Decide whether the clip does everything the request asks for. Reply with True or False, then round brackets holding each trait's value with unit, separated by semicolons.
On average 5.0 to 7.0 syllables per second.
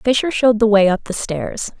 True (5.3 syllables/s)